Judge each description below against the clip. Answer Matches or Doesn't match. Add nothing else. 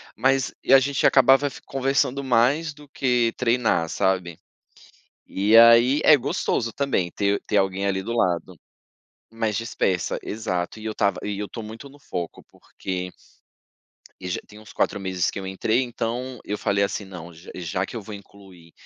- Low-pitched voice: Matches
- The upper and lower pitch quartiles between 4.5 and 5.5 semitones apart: Matches